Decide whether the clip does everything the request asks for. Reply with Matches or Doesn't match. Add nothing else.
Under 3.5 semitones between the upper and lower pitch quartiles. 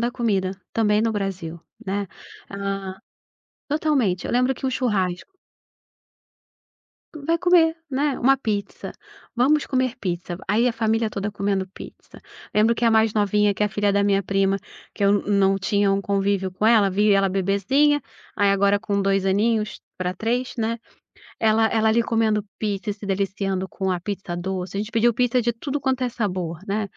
Matches